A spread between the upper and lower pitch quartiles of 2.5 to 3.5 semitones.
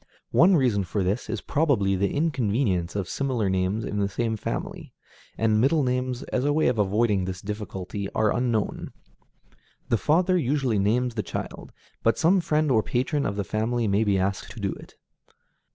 No: average, 4.6 semitones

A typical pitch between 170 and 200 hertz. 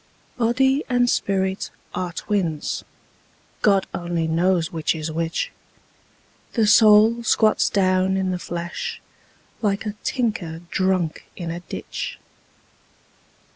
Yes: high, 190 Hz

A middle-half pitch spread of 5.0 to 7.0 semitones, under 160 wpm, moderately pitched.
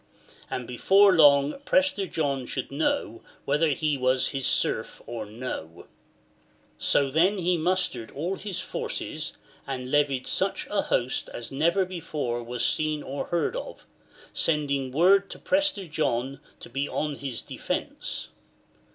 Yes: wide, 5.6 semitones; average, 145 wpm; medium, 145 Hz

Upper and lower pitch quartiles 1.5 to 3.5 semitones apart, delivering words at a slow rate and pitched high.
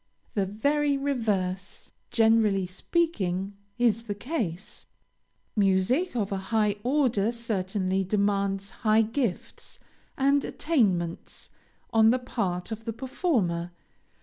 No: average, 4.4 semitones; slow, 105 wpm; high, 215 Hz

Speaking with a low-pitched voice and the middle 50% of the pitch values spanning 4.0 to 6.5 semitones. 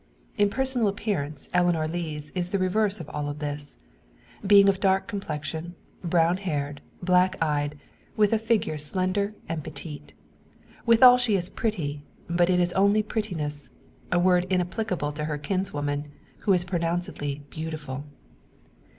No: medium, 175 Hz; average, 4.8 semitones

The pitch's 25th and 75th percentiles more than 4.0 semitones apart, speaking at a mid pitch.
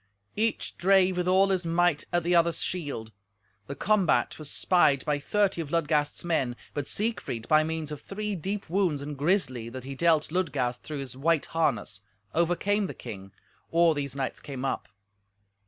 Yes: average, 4.6 semitones; medium, 160 Hz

